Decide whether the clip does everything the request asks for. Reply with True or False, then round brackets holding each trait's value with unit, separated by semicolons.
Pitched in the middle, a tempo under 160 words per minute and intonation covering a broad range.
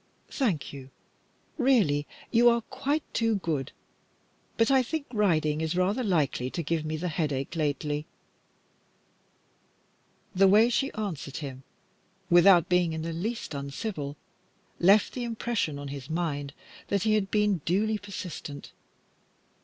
True (175 Hz; 135 wpm; 6.5 semitones)